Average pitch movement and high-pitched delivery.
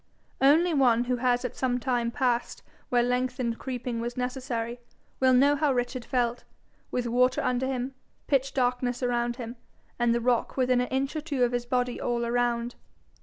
No: narrow, 1.3 semitones; very high, 250 Hz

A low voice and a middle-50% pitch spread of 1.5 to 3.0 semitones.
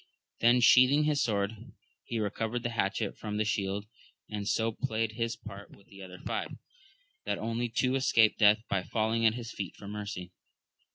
Yes: low, 110 Hz; narrow, 2.4 semitones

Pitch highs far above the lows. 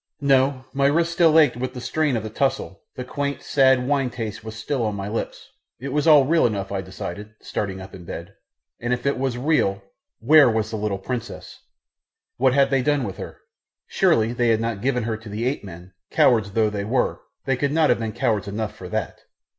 No: average, 4.4 semitones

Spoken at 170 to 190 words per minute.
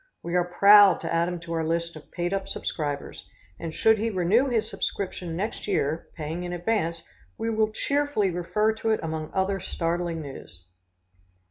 Yes: average, 175 wpm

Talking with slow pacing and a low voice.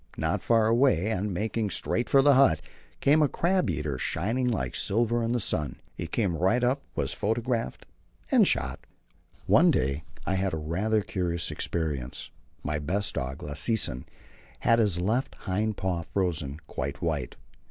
No: average, 160 wpm; very low, 95 Hz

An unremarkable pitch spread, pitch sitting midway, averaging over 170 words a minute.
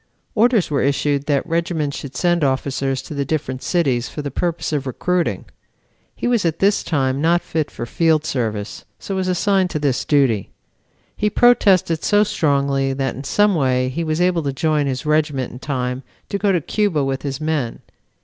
Yes: average, 4.4 semitones; medium, 150 Hz; average, 190 wpm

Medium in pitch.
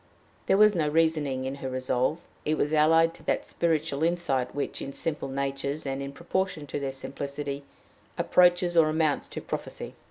Yes: medium, 150 Hz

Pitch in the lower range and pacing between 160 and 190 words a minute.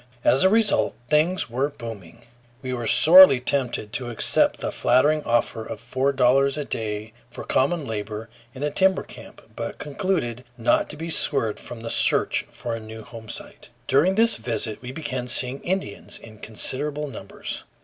Yes: low, 130 Hz; average, 170 wpm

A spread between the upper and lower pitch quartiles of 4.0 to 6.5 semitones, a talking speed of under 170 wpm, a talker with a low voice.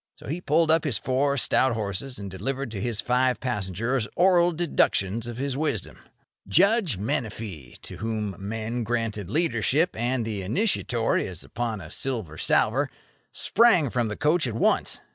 Yes: average, 4.9 semitones; average, 160 wpm; low, 120 Hz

